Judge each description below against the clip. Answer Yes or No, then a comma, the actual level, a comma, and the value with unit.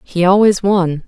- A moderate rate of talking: Yes, average, 170 wpm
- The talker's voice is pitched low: No, medium, 185 Hz